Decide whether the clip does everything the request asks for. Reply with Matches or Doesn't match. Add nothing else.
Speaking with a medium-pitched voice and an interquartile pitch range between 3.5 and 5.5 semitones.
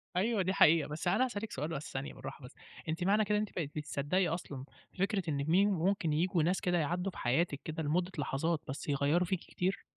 Matches